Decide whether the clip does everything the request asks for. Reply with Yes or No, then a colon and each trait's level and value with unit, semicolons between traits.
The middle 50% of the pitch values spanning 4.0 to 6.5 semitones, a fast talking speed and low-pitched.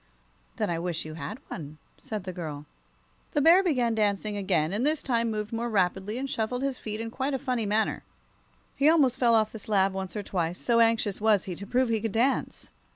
No: average, 4.3 semitones; fast, 220 wpm; high, 220 Hz